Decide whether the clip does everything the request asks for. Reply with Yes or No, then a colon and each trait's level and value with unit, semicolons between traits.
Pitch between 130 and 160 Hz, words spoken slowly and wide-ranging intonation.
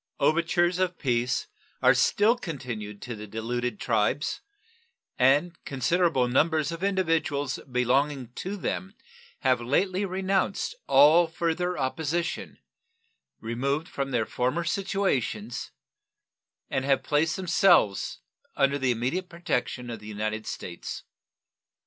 Yes: medium, 140 Hz; slow, 110 wpm; wide, 6.0 semitones